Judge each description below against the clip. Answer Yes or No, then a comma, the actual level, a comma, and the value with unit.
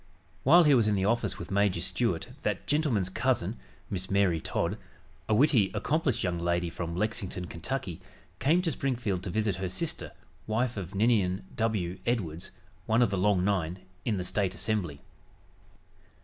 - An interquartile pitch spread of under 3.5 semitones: No, average, 4.7 semitones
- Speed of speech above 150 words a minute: Yes, average, 165 wpm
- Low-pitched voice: Yes, low, 100 Hz